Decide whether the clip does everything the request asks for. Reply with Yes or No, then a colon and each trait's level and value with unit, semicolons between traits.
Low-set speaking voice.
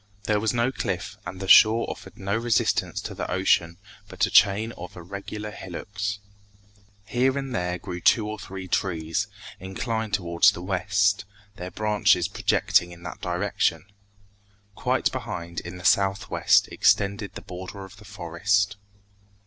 Yes: low, 100 Hz